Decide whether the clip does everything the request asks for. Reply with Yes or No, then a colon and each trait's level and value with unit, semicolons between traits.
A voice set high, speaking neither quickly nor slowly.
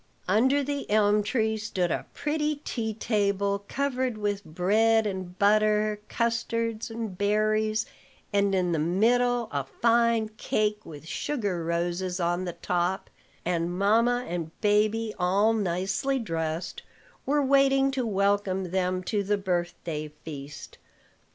No: high, 205 Hz; slow, 130 wpm